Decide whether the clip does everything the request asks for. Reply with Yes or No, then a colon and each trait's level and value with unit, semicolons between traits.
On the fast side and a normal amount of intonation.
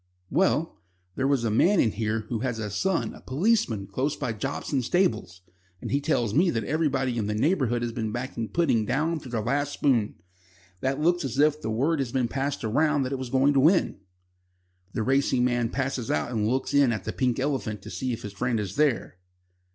Yes: fast, 210 wpm; average, 4.2 semitones